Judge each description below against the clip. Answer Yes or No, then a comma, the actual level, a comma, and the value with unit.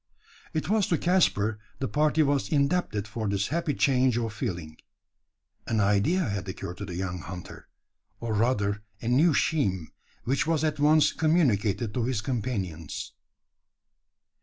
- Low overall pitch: Yes, low, 120 Hz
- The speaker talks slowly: No, average, 145 wpm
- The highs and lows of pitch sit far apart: Yes, wide, 6.9 semitones